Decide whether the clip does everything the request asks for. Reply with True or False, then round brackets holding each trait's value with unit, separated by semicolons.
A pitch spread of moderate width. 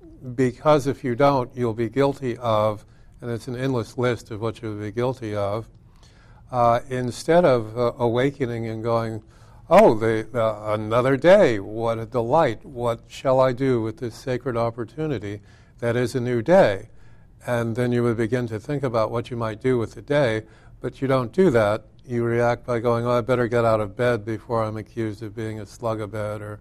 False (2.1 semitones)